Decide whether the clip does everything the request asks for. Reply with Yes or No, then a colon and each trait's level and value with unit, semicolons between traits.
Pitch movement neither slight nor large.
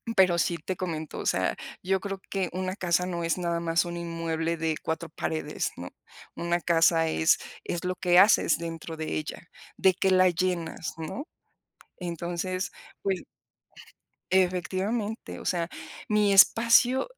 No: narrow, 2.1 semitones